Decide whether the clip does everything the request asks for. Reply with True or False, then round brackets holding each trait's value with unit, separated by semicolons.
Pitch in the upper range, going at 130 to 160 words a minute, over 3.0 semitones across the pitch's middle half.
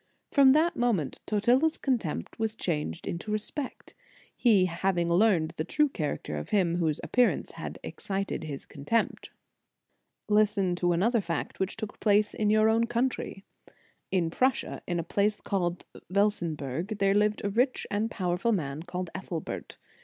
True (200 Hz; 155 wpm; 4.4 semitones)